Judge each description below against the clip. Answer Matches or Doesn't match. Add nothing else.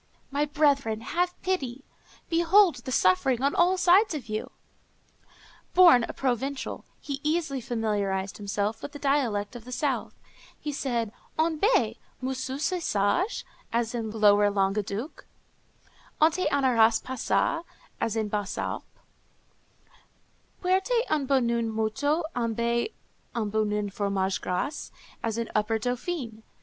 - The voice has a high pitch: Matches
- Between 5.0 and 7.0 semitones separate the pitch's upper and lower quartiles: Matches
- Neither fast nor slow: Doesn't match